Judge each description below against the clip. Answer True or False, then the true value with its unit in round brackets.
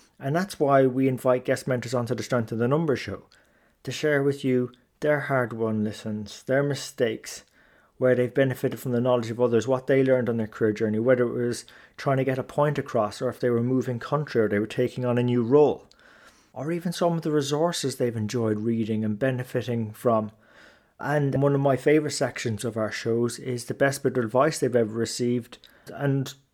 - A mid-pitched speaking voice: False (125 Hz)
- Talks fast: True (210 wpm)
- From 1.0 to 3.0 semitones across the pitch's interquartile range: True (2.6 semitones)